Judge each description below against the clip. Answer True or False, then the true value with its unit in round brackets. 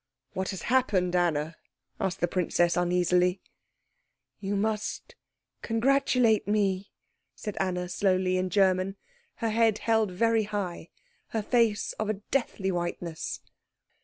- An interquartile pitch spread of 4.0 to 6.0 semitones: False (3.4 semitones)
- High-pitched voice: True (195 Hz)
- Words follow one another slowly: True (120 wpm)